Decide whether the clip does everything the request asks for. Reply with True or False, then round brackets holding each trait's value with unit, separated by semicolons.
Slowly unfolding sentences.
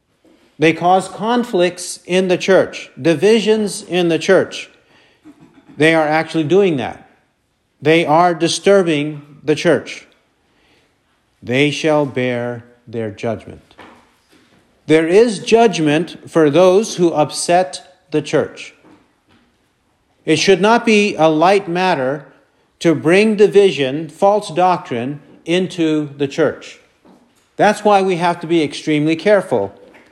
True (115 wpm)